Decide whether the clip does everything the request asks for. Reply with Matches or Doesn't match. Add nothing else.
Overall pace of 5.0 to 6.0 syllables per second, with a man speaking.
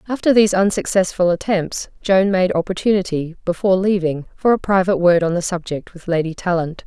Doesn't match